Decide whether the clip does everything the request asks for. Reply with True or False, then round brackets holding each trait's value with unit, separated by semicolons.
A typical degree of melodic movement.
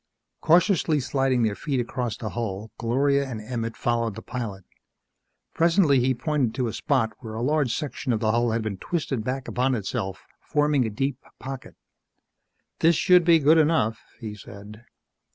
True (4.3 semitones)